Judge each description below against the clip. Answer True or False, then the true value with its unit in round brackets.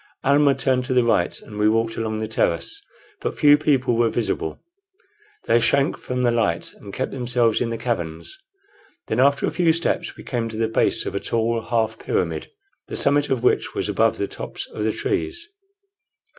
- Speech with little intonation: False (3.3 semitones)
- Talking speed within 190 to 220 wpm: True (195 wpm)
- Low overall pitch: True (120 Hz)